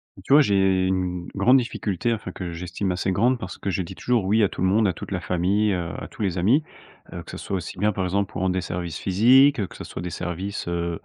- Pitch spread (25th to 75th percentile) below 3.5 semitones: Yes, average, 2.9 semitones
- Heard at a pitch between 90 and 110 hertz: Yes, very low, 95 Hz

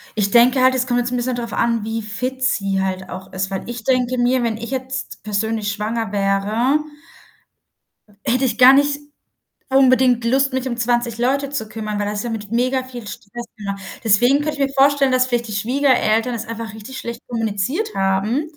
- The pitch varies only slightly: No, average, 3.3 semitones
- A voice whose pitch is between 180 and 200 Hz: No, high, 240 Hz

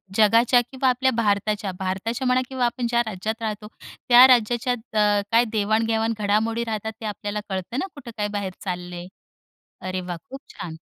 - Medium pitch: No, high, 220 Hz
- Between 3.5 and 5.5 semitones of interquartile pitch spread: No, average, 2.8 semitones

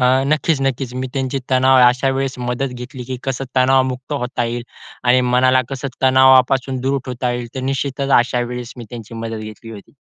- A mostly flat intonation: Yes, narrow, 1.5 semitones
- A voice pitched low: Yes, low, 130 Hz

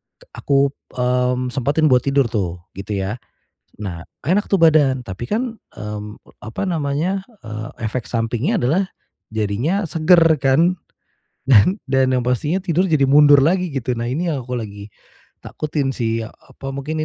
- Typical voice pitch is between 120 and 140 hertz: Yes, low, 135 Hz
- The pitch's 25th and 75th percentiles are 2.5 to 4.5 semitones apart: No, wide, 5.4 semitones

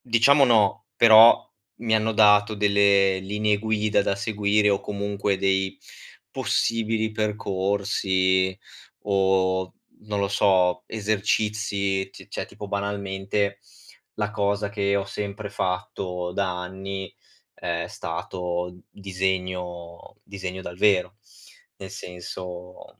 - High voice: No, low, 100 Hz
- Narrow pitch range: Yes, narrow, 1.9 semitones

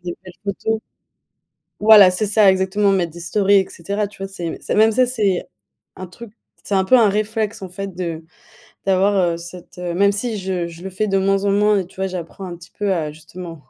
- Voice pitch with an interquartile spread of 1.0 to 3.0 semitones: Yes, narrow, 2.5 semitones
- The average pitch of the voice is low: No, high, 195 Hz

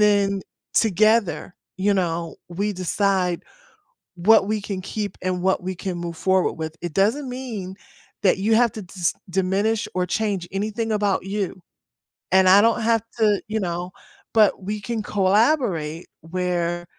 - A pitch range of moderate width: Yes, average, 3.0 semitones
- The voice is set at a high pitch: Yes, high, 195 Hz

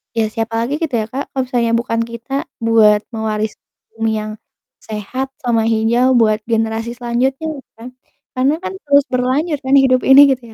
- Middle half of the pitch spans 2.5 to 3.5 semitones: Yes, average, 2.8 semitones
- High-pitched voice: Yes, high, 235 Hz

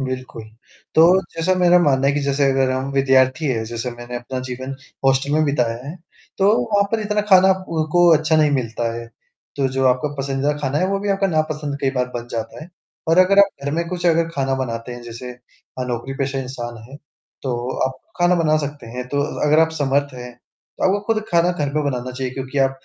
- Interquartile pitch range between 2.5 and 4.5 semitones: Yes, average, 4.1 semitones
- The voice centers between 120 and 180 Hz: Yes, low, 135 Hz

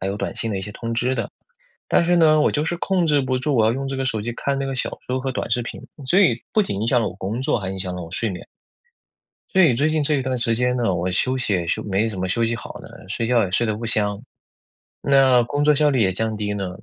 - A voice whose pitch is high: No, low, 120 Hz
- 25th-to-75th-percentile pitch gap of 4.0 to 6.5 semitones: Yes, average, 4.8 semitones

